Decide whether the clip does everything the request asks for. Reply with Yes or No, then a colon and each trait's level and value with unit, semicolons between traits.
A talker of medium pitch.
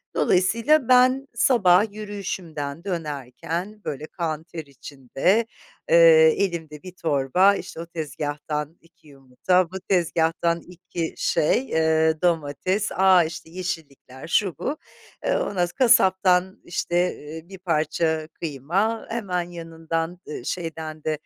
Yes: medium, 170 Hz